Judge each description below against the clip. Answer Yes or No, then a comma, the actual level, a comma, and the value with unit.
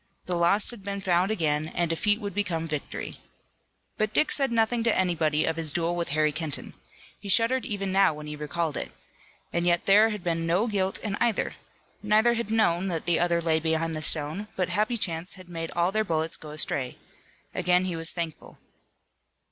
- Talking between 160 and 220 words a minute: Yes, average, 195 wpm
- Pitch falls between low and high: Yes, medium, 175 Hz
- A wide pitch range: No, average, 4.1 semitones